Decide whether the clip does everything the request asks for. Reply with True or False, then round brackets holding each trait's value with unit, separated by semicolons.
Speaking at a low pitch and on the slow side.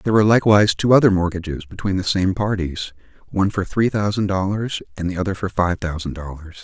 False (95 Hz; 200 wpm)